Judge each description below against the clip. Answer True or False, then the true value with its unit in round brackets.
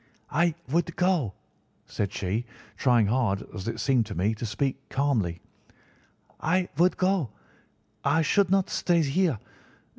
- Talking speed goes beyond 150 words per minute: False (140 wpm)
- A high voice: False (135 Hz)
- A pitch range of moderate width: False (8.0 semitones)